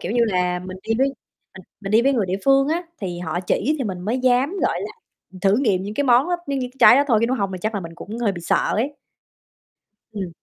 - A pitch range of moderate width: No, wide, 5.7 semitones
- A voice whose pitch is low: No, high, 215 Hz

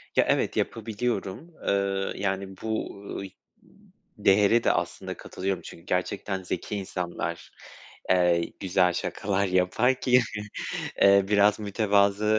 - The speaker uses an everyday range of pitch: No, narrow, 2.0 semitones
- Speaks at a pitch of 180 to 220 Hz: No, low, 100 Hz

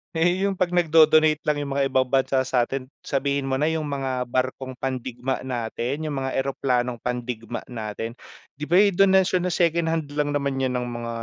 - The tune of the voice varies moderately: Yes, average, 3.9 semitones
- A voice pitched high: No, low, 135 Hz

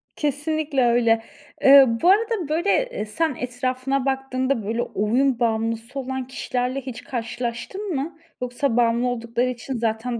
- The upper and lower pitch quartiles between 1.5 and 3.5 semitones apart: Yes, average, 2.8 semitones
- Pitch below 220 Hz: No, very high, 255 Hz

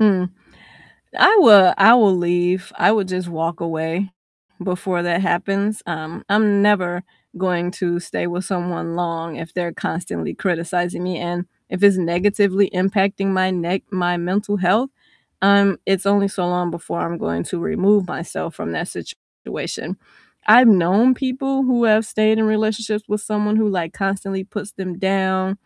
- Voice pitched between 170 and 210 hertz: Yes, medium, 185 Hz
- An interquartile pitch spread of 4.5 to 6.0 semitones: No, average, 2.8 semitones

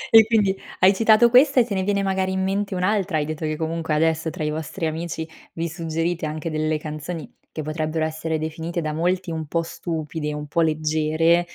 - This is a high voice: No, medium, 165 Hz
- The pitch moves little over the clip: No, average, 3.2 semitones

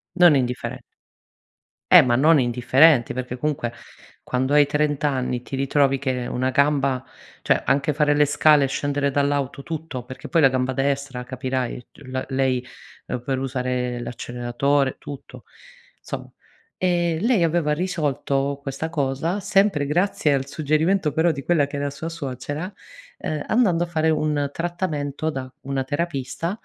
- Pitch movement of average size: Yes, average, 3.2 semitones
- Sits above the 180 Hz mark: No, medium, 140 Hz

